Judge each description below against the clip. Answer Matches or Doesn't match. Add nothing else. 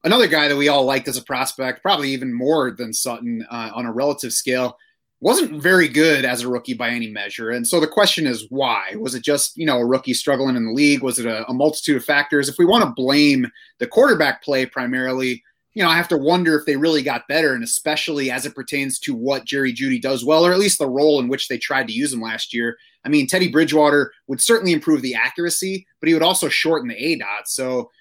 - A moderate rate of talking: Doesn't match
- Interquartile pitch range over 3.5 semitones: Matches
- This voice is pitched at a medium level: Matches